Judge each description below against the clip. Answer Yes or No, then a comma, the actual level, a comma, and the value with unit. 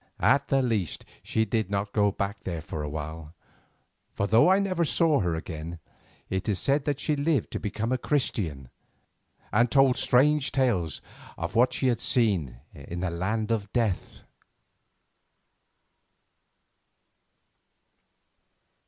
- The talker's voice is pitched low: Yes, low, 110 Hz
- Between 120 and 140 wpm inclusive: Yes, slow, 135 wpm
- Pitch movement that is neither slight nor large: No, wide, 6.9 semitones